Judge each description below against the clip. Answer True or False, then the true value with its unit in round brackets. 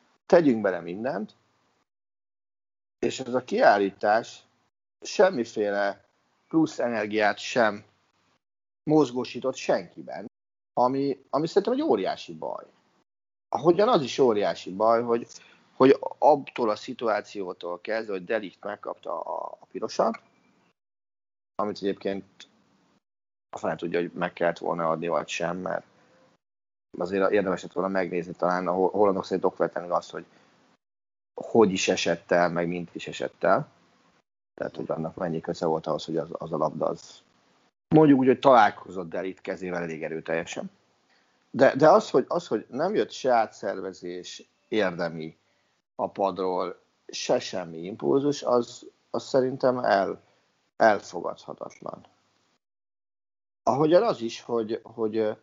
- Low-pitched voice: True (100 Hz)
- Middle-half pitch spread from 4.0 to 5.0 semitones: True (4.5 semitones)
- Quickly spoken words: False (125 wpm)